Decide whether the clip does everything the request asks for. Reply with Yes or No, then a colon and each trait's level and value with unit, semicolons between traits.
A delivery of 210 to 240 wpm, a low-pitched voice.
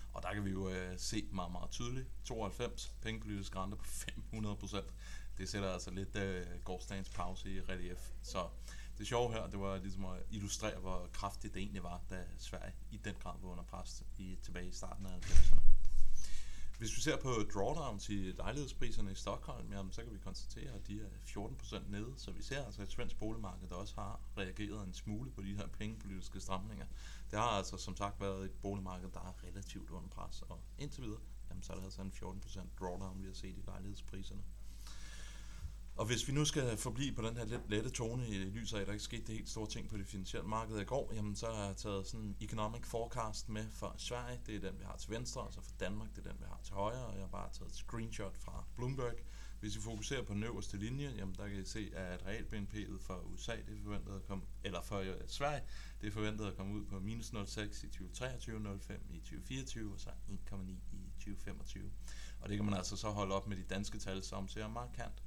Yes: fast, 225 wpm; low, 100 Hz